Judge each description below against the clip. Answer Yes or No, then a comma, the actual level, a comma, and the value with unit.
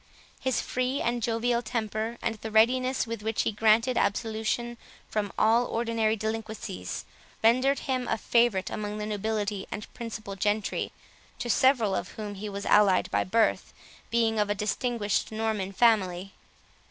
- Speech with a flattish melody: Yes, narrow, 2.1 semitones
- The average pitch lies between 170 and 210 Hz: No, high, 220 Hz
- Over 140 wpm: Yes, average, 150 wpm